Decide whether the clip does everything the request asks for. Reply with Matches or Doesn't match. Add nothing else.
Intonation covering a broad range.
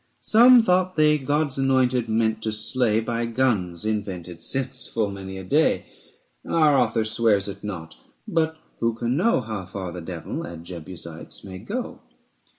Matches